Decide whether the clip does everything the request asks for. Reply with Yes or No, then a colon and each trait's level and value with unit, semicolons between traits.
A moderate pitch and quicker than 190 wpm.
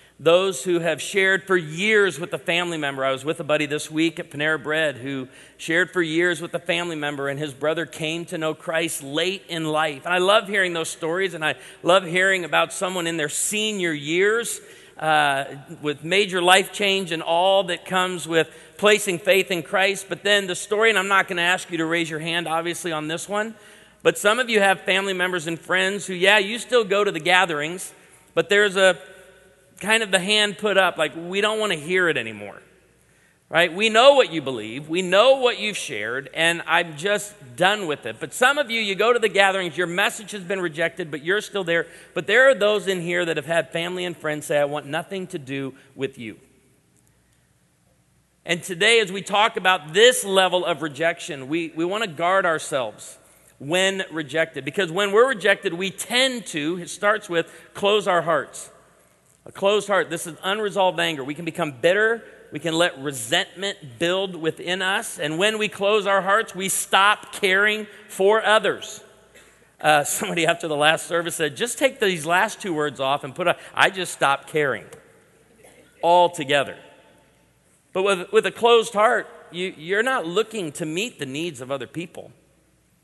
Yes: medium, 180 Hz; average, 200 wpm